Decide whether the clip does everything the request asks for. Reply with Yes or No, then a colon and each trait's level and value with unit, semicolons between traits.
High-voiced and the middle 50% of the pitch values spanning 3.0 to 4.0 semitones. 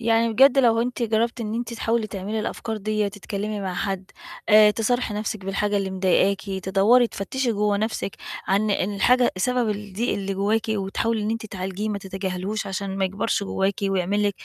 No: high, 210 Hz; narrow, 2.5 semitones